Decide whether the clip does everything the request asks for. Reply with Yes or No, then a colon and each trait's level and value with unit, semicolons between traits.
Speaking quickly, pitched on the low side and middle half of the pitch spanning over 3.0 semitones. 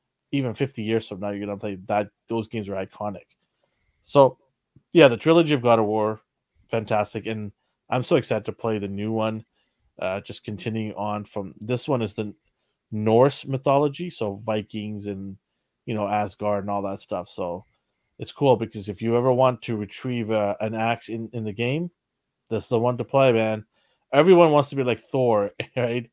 No: average, 190 wpm; low, 110 Hz; average, 3.4 semitones